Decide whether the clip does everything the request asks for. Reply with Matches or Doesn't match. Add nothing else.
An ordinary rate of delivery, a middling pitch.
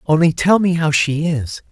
Doesn't match